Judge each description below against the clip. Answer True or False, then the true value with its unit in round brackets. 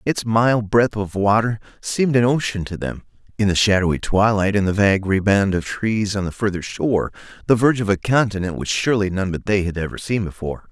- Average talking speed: False (215 wpm)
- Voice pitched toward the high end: False (105 Hz)